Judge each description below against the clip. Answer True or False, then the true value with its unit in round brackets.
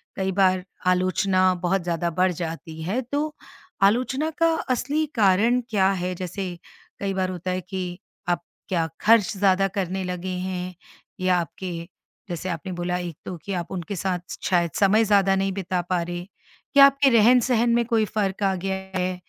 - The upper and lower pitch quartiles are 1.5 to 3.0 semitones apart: True (2.4 semitones)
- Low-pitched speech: False (185 Hz)